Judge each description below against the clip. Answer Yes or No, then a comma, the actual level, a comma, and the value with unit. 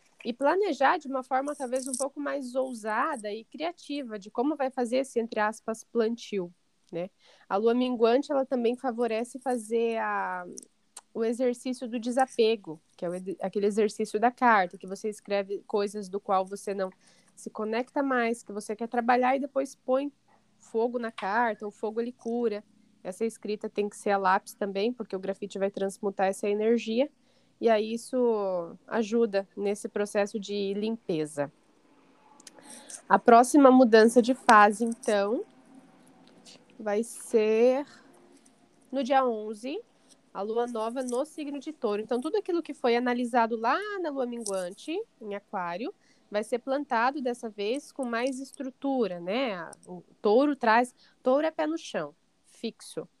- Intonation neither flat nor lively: Yes, average, 3.9 semitones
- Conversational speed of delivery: Yes, average, 155 wpm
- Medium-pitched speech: No, high, 230 Hz